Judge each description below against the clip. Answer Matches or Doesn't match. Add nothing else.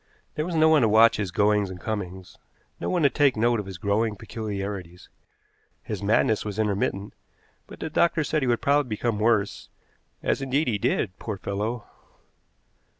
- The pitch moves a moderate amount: Matches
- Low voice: Matches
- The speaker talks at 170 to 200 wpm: Matches